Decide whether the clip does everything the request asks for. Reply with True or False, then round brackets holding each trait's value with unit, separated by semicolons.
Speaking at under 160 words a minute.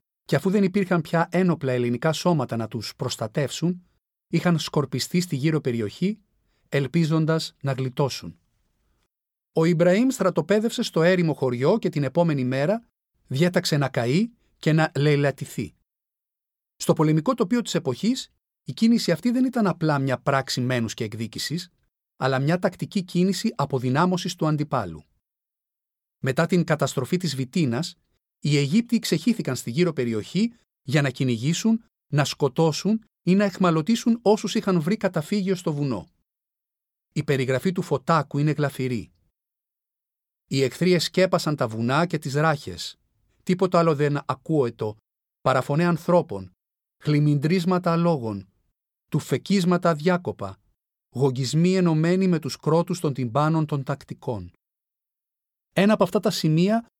True (130 wpm)